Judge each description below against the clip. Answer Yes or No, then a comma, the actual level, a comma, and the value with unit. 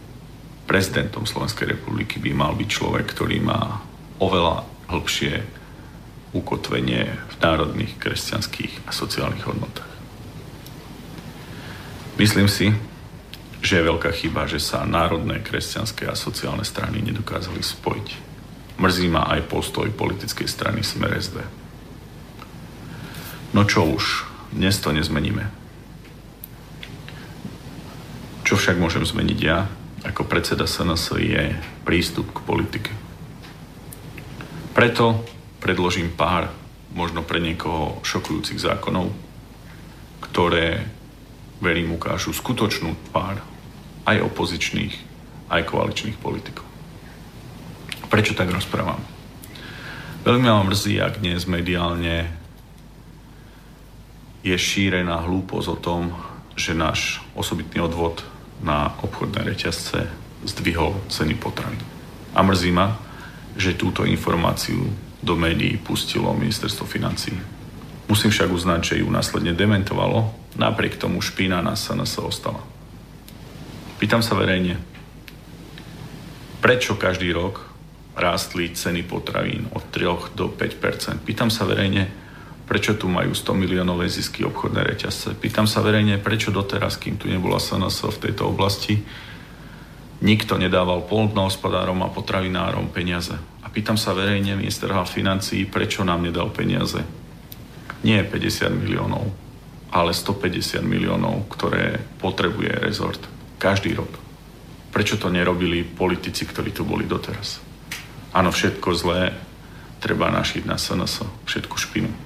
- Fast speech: No, slow, 110 wpm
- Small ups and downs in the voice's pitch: No, average, 3.8 semitones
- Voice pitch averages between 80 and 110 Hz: Yes, low, 100 Hz